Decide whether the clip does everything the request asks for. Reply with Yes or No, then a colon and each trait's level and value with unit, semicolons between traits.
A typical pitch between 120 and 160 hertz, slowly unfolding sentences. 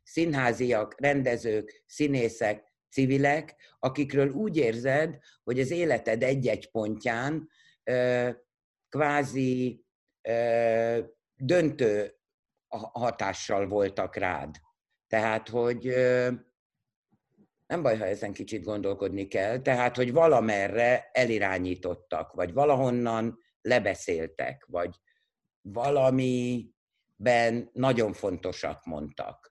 Yes: low, 125 Hz; slow, 85 wpm